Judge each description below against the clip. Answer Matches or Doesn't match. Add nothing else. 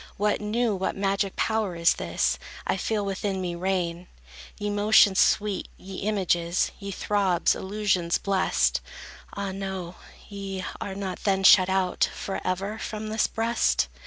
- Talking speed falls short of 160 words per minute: Matches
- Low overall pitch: Doesn't match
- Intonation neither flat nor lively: Doesn't match